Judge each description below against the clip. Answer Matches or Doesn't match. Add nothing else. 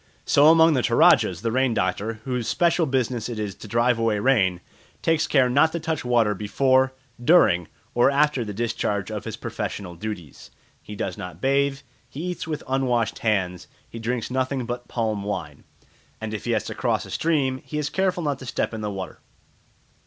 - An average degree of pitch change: Matches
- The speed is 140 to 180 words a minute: Doesn't match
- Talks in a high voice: Doesn't match